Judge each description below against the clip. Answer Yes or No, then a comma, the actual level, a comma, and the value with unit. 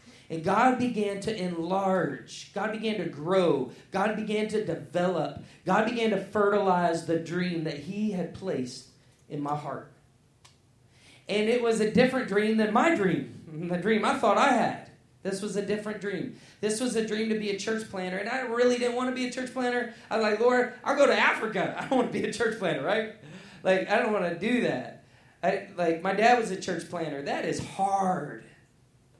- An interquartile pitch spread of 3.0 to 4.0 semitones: No, average, 5.2 semitones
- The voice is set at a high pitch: Yes, high, 195 Hz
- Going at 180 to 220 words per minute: Yes, fast, 205 wpm